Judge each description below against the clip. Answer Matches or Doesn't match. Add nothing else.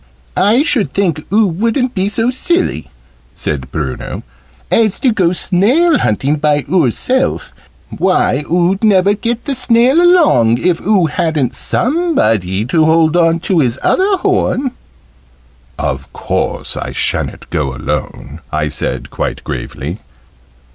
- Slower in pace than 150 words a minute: Matches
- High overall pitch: Doesn't match